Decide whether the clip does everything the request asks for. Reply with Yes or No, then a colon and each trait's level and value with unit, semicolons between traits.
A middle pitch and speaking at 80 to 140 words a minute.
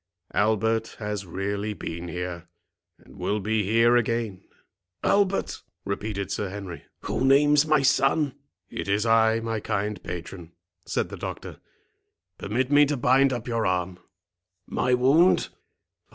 No: low, 110 Hz; slow, 135 wpm